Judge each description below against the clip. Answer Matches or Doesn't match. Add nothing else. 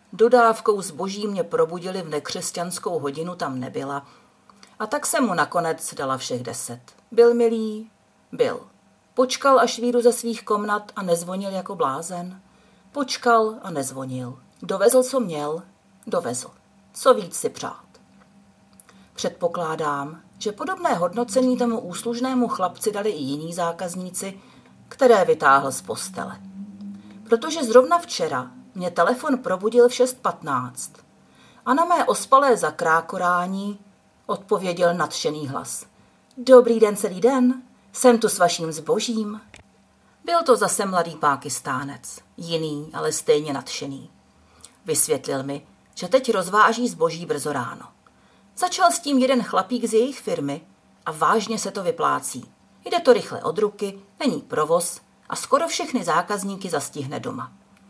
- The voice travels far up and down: Matches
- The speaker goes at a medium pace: Matches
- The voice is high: Matches